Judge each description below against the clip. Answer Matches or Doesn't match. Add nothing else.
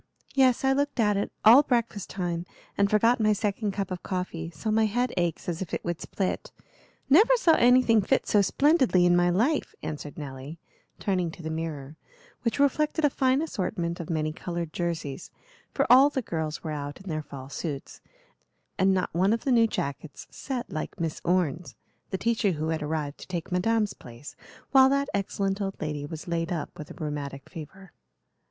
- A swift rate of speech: Doesn't match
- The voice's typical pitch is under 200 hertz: Matches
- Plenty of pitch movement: Matches